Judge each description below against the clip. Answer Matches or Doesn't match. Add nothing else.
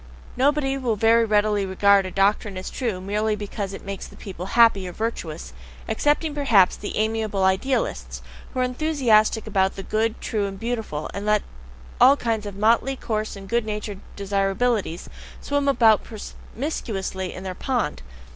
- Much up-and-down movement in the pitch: Doesn't match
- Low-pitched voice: Doesn't match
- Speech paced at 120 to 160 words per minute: Matches